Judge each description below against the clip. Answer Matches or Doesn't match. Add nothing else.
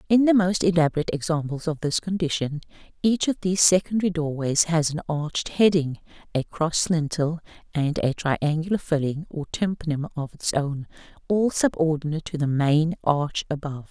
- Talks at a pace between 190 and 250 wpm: Doesn't match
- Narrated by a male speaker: Doesn't match